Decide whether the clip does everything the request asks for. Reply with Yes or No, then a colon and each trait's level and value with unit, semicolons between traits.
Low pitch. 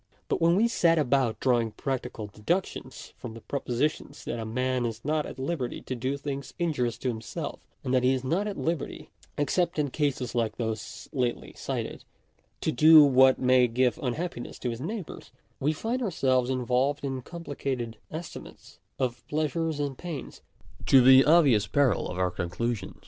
Yes: low, 130 Hz